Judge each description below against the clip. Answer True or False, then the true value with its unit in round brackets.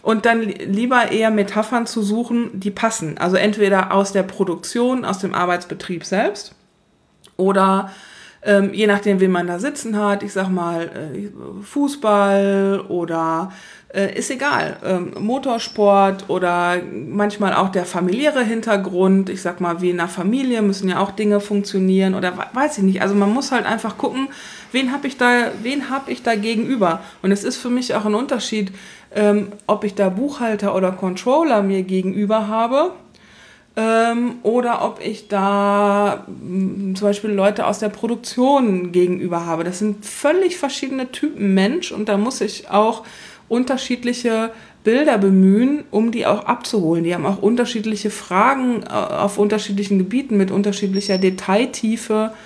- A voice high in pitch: True (205 Hz)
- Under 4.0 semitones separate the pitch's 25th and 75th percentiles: True (3.1 semitones)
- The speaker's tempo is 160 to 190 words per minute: False (150 wpm)